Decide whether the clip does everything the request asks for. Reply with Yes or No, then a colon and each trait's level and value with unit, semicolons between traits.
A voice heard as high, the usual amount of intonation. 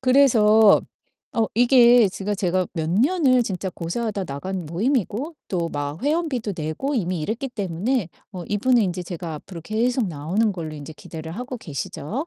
No: high, 205 Hz; wide, 6.3 semitones